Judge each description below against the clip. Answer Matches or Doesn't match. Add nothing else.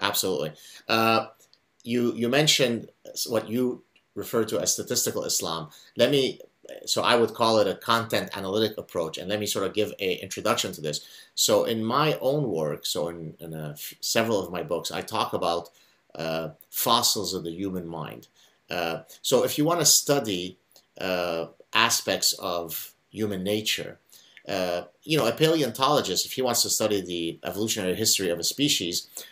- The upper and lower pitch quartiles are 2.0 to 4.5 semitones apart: Doesn't match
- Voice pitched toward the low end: Matches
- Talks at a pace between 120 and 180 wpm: Matches